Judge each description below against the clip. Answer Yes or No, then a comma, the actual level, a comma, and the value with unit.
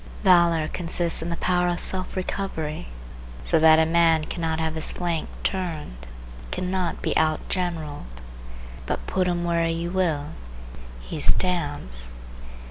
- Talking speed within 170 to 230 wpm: No, slow, 135 wpm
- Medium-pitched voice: Yes, medium, 165 Hz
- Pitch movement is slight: Yes, narrow, 2.2 semitones